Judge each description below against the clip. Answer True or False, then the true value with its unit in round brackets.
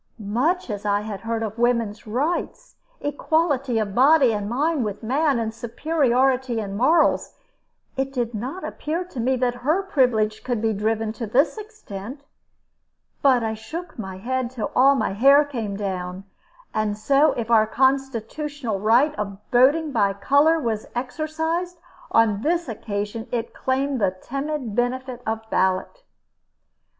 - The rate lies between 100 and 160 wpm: True (150 wpm)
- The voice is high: True (245 Hz)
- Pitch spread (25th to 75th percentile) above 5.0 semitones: False (4.7 semitones)